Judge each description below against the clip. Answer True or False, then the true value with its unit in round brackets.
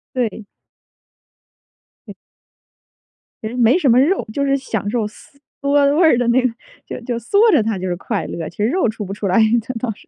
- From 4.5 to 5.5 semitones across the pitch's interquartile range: True (4.8 semitones)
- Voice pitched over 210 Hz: True (240 Hz)